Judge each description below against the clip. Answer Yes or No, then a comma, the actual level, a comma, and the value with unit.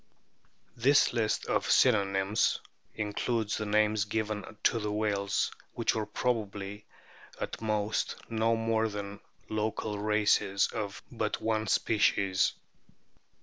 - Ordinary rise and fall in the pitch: No, narrow, 1.4 semitones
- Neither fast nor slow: No, slow, 110 wpm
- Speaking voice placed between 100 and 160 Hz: Yes, low, 105 Hz